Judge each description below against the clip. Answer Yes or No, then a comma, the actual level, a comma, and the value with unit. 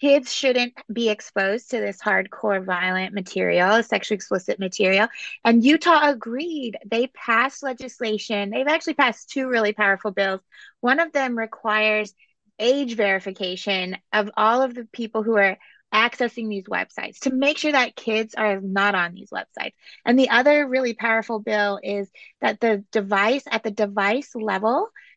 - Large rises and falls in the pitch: No, average, 4.1 semitones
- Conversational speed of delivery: Yes, average, 155 wpm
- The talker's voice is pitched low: No, high, 225 Hz